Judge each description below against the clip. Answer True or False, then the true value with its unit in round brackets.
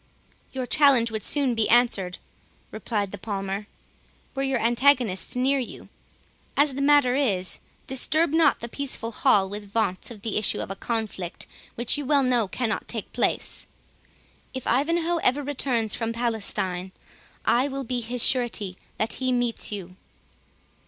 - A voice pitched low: False (235 Hz)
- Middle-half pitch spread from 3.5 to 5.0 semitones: True (4.4 semitones)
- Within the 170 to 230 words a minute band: False (150 wpm)